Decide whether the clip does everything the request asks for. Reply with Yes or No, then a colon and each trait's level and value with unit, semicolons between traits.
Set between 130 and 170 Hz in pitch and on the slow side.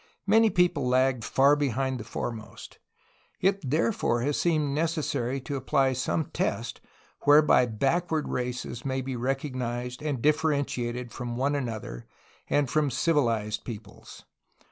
Yes: low, 135 Hz; slow, 130 wpm